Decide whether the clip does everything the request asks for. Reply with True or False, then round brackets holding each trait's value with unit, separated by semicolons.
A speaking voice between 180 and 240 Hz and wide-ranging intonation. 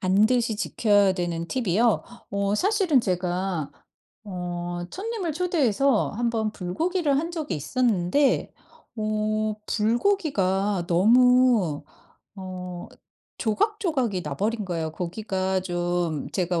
True (210 Hz; 5.8 semitones)